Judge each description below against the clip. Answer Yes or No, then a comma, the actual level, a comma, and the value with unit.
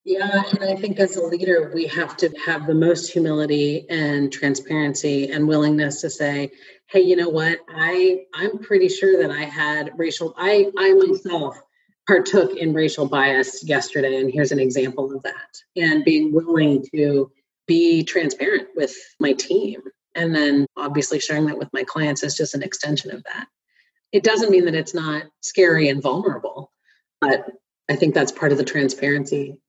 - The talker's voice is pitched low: No, medium, 160 Hz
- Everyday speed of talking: Yes, average, 175 wpm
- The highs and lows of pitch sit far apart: No, average, 4.8 semitones